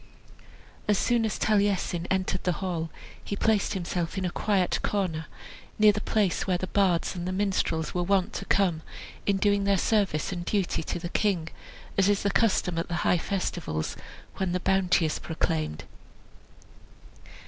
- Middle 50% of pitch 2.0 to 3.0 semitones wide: Yes, narrow, 2.6 semitones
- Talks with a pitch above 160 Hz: Yes, medium, 185 Hz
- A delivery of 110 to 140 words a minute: No, average, 170 wpm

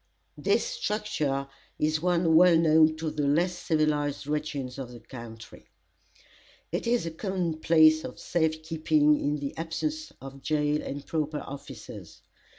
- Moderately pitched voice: Yes, medium, 155 Hz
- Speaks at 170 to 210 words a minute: No, average, 145 wpm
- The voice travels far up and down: No, narrow, 2.4 semitones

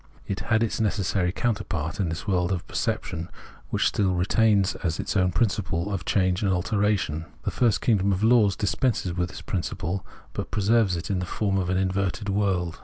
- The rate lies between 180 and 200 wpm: Yes, average, 195 wpm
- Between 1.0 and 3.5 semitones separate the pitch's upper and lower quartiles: Yes, average, 2.7 semitones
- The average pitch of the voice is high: No, very low, 95 Hz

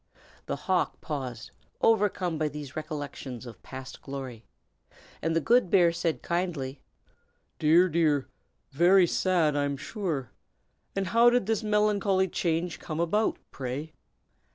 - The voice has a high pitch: No, medium, 165 Hz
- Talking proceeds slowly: Yes, slow, 130 wpm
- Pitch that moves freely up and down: No, average, 4.9 semitones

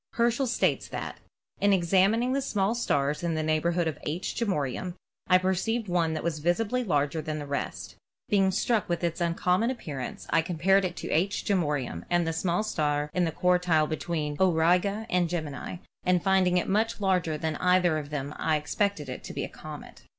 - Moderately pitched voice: Yes, medium, 175 Hz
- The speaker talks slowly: No, average, 195 wpm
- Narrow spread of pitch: No, average, 3.6 semitones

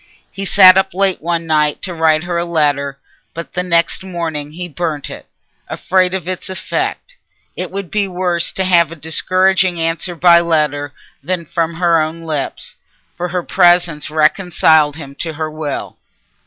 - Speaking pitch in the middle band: Yes, medium, 170 Hz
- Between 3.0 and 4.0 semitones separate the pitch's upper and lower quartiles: No, narrow, 2.6 semitones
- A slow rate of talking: No, average, 170 wpm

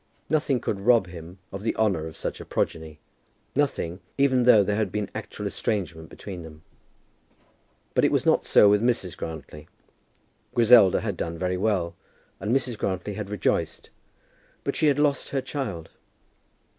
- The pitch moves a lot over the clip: Yes, wide, 6.0 semitones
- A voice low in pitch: Yes, low, 100 Hz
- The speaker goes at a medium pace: Yes, average, 160 wpm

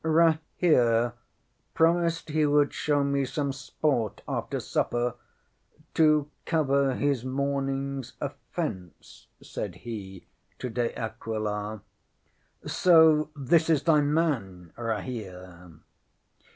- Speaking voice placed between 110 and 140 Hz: Yes, low, 135 Hz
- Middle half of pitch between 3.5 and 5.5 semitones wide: Yes, average, 5.2 semitones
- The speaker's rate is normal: No, slow, 95 wpm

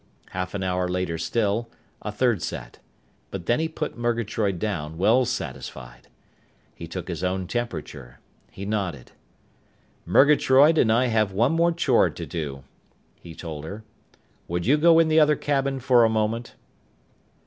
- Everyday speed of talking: Yes, average, 155 wpm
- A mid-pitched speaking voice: No, low, 110 Hz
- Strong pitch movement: Yes, wide, 6.0 semitones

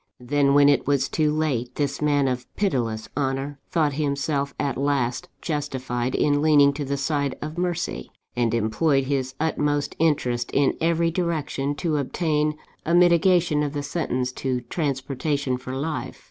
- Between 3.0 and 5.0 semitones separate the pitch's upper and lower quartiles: No, narrow, 2.6 semitones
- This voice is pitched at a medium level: Yes, medium, 145 Hz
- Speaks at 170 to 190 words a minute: No, average, 155 wpm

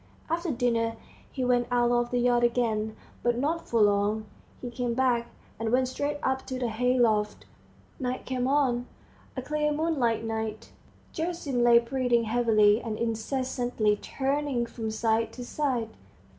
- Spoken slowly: No, average, 155 wpm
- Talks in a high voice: Yes, high, 240 Hz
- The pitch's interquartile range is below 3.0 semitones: Yes, narrow, 2.4 semitones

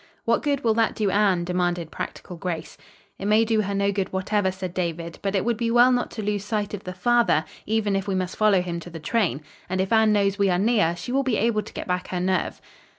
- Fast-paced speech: Yes, fast, 255 wpm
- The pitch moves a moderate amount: Yes, average, 3.4 semitones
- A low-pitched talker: No, high, 200 Hz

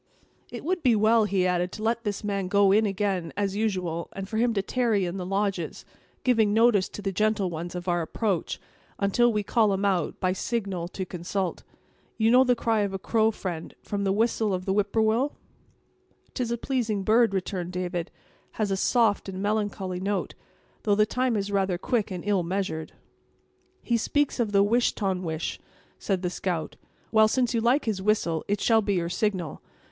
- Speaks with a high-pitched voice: Yes, high, 200 Hz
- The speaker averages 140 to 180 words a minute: No, average, 200 wpm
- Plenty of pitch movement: No, average, 3.1 semitones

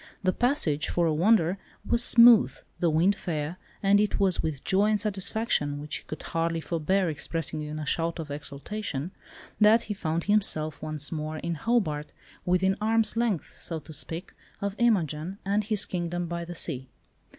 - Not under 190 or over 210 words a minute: No, average, 175 wpm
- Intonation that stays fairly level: No, average, 4.8 semitones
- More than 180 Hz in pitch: No, medium, 175 Hz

